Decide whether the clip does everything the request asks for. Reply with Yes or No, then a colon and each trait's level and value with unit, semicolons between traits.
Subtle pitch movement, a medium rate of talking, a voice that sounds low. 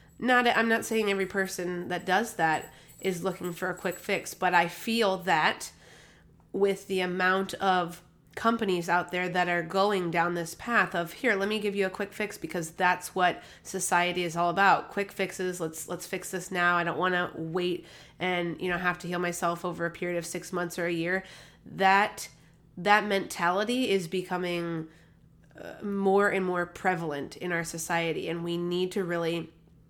No: narrow, 2.0 semitones; average, 185 wpm; medium, 180 Hz